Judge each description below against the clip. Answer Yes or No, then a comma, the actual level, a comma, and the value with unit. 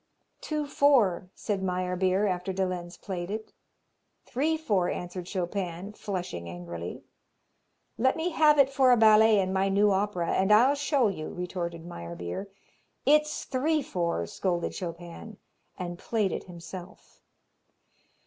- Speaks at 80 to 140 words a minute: Yes, slow, 135 wpm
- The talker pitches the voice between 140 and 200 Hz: Yes, high, 190 Hz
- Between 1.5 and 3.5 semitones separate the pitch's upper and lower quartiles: No, average, 4.4 semitones